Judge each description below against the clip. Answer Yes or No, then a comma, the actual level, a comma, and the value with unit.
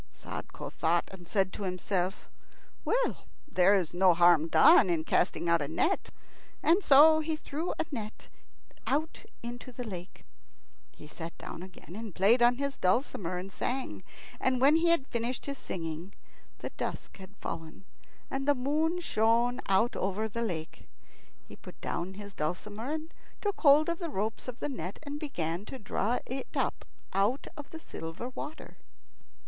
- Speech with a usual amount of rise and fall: No, wide, 7.5 semitones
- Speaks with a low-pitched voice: No, high, 220 Hz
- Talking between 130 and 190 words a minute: Yes, average, 165 wpm